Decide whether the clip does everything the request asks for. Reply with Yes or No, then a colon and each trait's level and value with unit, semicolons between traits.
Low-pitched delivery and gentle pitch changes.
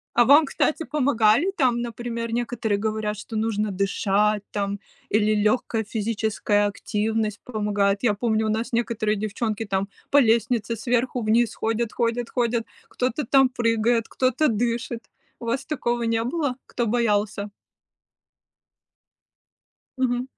No: high, 230 Hz; narrow, 2.2 semitones